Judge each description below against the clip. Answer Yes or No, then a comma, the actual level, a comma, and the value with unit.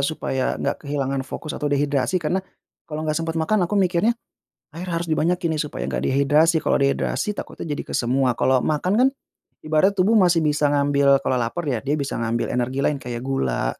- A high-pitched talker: No, medium, 150 Hz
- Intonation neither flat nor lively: Yes, average, 3.8 semitones